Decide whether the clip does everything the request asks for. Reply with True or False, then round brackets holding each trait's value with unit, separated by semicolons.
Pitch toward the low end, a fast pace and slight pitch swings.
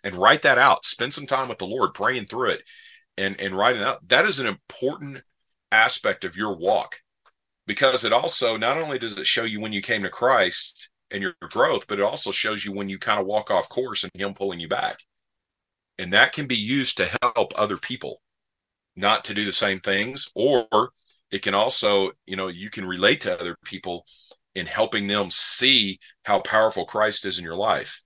True (105 Hz; 210 wpm; 2.2 semitones)